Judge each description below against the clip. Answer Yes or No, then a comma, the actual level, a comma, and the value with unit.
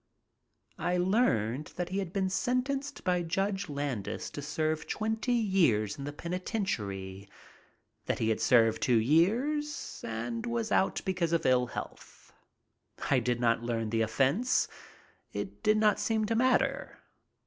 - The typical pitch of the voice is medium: Yes, medium, 175 Hz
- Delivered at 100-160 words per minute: Yes, average, 145 wpm